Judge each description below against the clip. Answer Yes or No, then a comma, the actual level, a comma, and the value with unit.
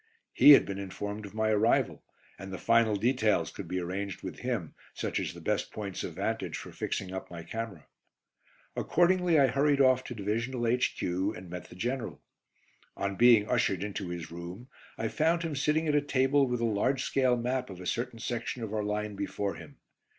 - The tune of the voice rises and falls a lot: No, average, 4.8 semitones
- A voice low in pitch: Yes, low, 110 Hz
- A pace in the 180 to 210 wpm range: Yes, average, 195 wpm